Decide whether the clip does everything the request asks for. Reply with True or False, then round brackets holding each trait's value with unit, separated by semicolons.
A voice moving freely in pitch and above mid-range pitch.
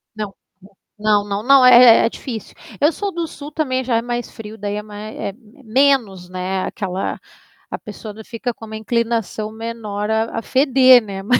False (3.3 semitones; 225 Hz)